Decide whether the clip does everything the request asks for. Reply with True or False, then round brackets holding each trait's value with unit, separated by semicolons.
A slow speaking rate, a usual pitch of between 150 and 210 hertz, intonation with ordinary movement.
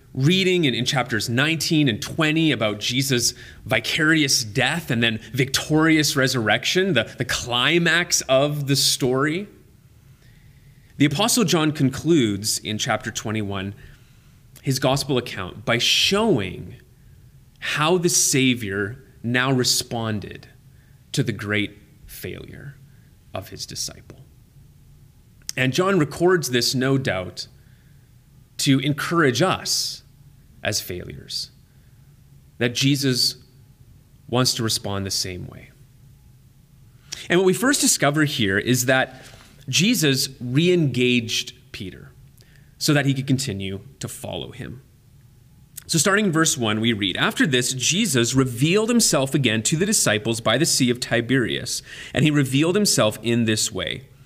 False (125 wpm; 130 Hz; 3.0 semitones)